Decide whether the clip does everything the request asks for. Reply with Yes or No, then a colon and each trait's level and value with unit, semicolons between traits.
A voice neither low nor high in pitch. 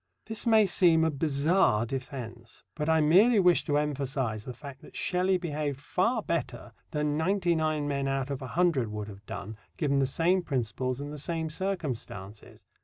Yes: medium, 150 Hz